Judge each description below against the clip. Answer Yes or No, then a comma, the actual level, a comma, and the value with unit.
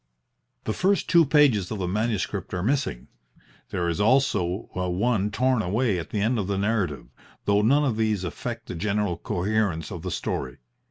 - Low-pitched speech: Yes, low, 105 Hz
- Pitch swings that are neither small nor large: Yes, average, 4.6 semitones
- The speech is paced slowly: No, average, 175 wpm